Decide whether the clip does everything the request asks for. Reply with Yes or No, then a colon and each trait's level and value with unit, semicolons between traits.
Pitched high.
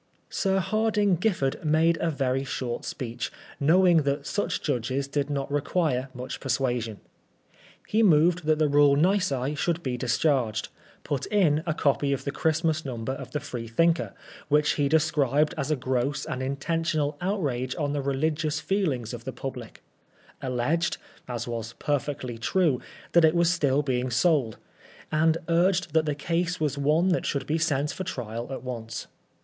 No: medium, 145 Hz